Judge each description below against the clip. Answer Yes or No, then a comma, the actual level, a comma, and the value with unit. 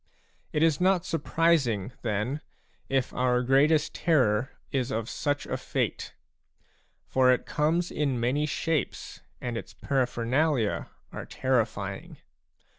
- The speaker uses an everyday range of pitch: Yes, average, 4.1 semitones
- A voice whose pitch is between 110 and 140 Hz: Yes, low, 135 Hz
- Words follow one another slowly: Yes, slow, 125 wpm